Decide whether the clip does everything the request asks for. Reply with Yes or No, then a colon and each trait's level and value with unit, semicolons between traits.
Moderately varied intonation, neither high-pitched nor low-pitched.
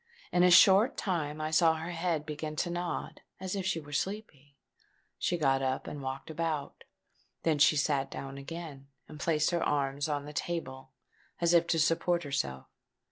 Yes: average, 3.4 semitones; medium, 155 Hz